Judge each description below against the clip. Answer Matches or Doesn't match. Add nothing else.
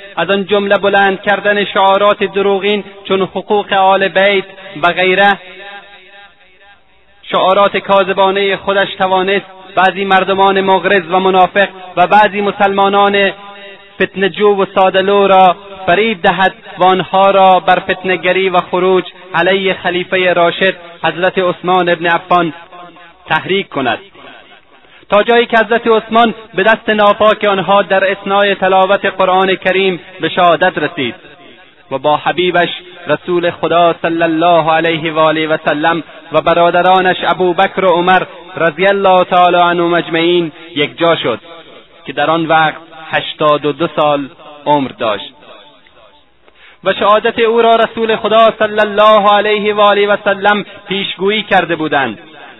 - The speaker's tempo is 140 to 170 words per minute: Doesn't match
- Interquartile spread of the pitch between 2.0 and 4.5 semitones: Matches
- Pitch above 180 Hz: Matches